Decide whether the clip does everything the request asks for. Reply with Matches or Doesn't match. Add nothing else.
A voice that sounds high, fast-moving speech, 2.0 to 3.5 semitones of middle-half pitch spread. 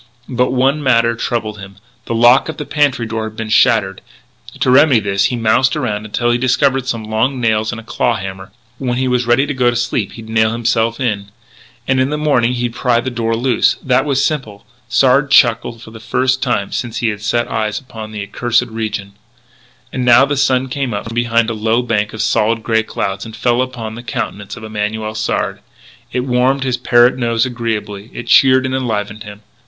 Doesn't match